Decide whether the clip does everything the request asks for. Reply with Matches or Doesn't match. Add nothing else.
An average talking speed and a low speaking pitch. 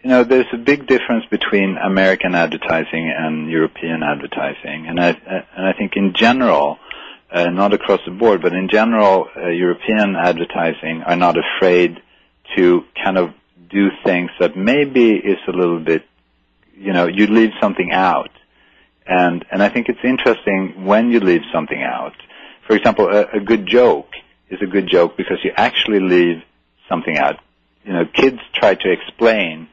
Matches